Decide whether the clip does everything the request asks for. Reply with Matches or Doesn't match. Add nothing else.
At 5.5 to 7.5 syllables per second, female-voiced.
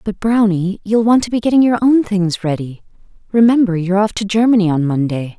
Matches